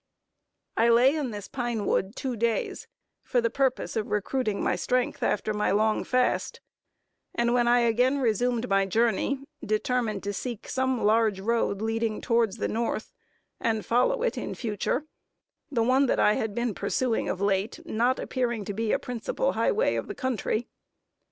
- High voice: Yes, high, 235 Hz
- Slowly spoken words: No, average, 170 wpm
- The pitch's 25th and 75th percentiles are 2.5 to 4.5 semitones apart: Yes, average, 2.8 semitones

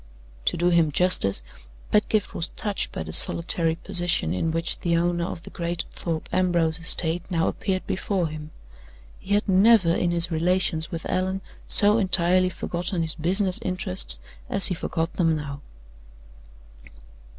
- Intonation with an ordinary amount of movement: No, narrow, 2.2 semitones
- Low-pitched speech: No, medium, 175 Hz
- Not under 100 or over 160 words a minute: Yes, average, 150 wpm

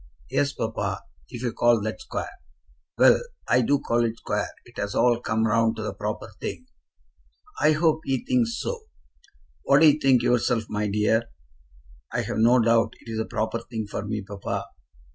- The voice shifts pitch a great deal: No, average, 3.8 semitones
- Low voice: Yes, low, 115 Hz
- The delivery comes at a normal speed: Yes, average, 175 wpm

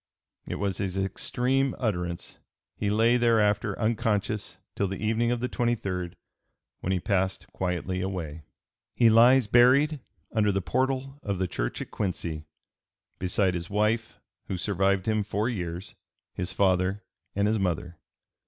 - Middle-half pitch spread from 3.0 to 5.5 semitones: Yes, average, 3.8 semitones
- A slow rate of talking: No, average, 145 wpm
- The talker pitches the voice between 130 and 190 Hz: No, low, 100 Hz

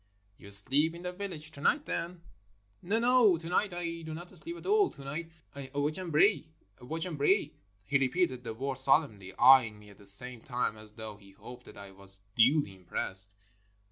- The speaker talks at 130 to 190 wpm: No, fast, 205 wpm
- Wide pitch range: Yes, wide, 8.0 semitones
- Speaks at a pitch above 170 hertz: No, medium, 140 Hz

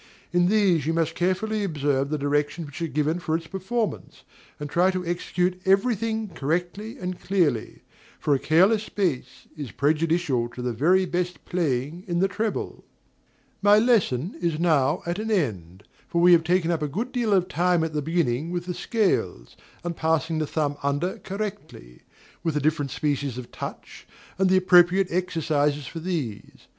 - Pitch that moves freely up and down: No, average, 4.1 semitones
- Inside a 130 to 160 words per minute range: No, average, 175 wpm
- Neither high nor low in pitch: Yes, medium, 170 Hz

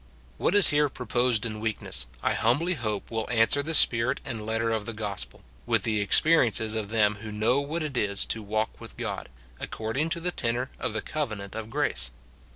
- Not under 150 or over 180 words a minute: No, average, 195 wpm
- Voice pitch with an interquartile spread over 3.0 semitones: Yes, average, 3.8 semitones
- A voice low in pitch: Yes, low, 115 Hz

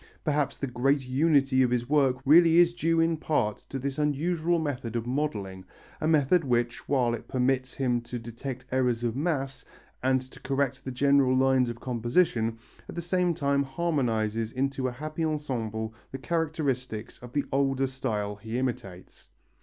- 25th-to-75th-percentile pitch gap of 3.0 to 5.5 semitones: Yes, average, 3.6 semitones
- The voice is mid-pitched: No, low, 130 Hz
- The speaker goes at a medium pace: Yes, average, 170 wpm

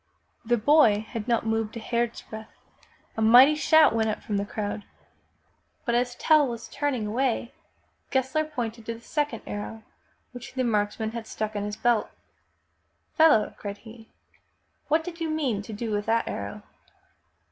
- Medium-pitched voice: No, high, 230 Hz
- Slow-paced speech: No, average, 170 wpm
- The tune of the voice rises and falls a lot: No, average, 3.3 semitones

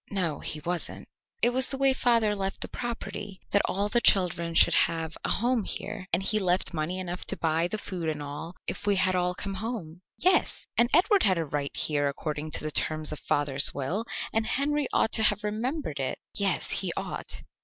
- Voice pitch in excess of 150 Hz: Yes, medium, 185 Hz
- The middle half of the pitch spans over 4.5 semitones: Yes, wide, 5.6 semitones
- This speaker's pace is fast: Yes, fast, 210 wpm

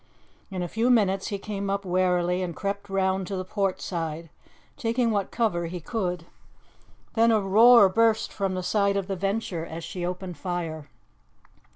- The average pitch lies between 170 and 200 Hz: Yes, high, 190 Hz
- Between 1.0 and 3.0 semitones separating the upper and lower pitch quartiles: Yes, narrow, 2.5 semitones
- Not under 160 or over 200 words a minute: Yes, average, 175 wpm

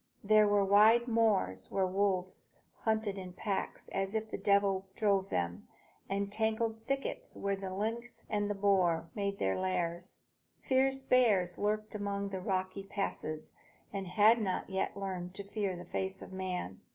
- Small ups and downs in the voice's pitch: Yes, narrow, 2.3 semitones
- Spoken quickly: No, average, 165 wpm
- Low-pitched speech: No, high, 200 Hz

